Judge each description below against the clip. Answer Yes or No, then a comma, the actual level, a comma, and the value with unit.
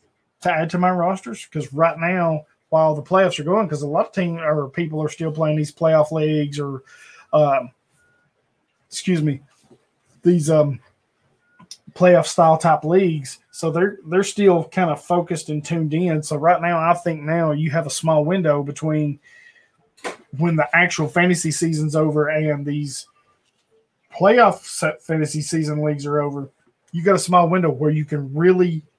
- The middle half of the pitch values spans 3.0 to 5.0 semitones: No, narrow, 2.6 semitones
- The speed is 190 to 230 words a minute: No, average, 170 wpm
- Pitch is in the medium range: Yes, medium, 160 Hz